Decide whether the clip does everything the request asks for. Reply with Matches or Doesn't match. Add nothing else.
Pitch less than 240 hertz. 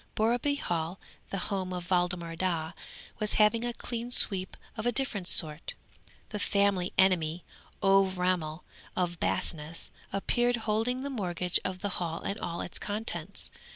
Matches